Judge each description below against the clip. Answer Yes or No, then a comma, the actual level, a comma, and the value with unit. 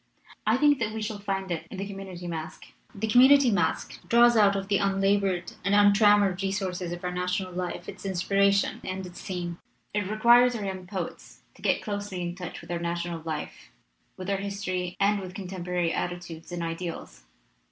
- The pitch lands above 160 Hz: Yes, high, 190 Hz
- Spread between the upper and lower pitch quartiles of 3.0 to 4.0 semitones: No, narrow, 2.4 semitones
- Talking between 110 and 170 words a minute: No, average, 190 wpm